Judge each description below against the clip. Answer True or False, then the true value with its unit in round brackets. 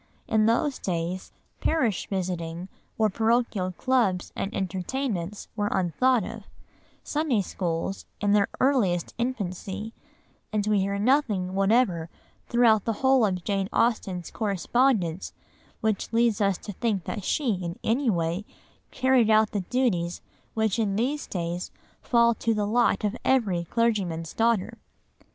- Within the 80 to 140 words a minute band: True (135 wpm)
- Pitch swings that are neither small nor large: True (4.2 semitones)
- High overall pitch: True (210 Hz)